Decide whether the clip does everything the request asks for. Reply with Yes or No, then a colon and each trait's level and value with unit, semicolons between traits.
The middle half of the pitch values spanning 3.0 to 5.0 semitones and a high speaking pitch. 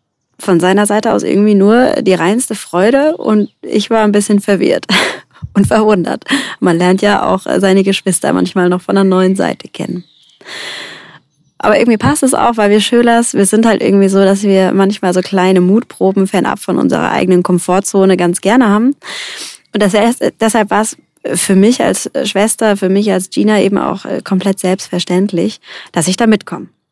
No: narrow, 2.5 semitones; high, 200 Hz